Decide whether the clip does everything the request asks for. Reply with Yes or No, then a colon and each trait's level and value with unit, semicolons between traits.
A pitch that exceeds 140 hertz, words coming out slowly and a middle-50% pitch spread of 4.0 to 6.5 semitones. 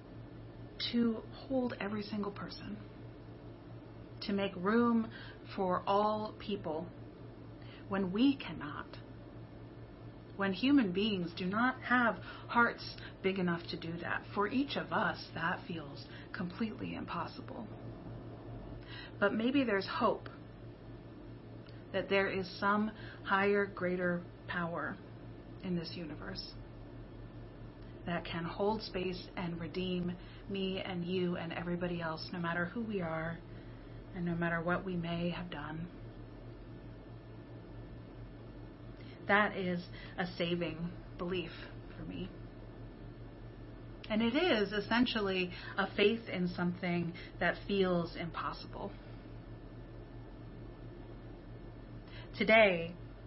No: high, 190 Hz; slow, 105 wpm; average, 3.2 semitones